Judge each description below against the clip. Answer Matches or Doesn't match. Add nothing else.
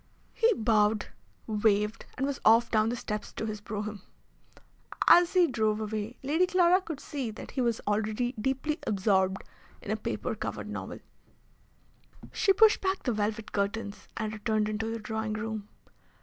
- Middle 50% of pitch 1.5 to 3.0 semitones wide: Doesn't match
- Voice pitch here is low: Doesn't match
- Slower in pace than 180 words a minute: Matches